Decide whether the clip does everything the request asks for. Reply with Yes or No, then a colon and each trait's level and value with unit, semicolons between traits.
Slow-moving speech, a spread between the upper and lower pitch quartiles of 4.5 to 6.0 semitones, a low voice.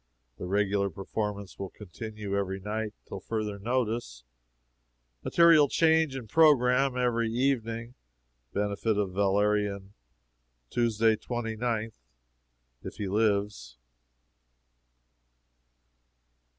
No: slow, 85 wpm; average, 3.1 semitones; low, 110 Hz